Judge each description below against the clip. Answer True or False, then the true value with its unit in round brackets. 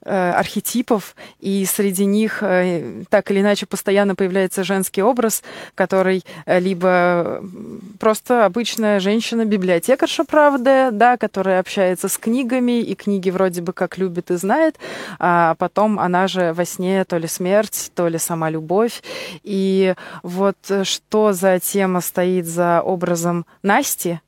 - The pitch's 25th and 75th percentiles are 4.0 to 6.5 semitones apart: False (2.7 semitones)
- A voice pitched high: True (195 Hz)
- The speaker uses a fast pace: False (130 wpm)